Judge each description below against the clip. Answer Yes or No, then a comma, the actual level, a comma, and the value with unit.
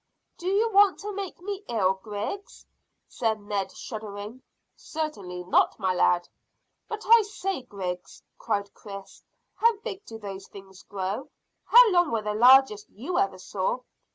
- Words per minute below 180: Yes, average, 150 wpm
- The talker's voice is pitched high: Yes, high, 220 Hz